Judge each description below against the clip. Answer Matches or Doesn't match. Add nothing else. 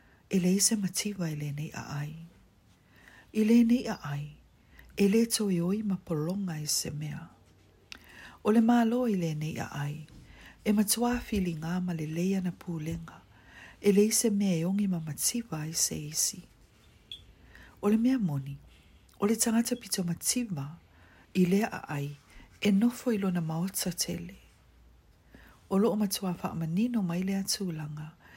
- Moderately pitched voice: Matches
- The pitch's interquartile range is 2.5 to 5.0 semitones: Doesn't match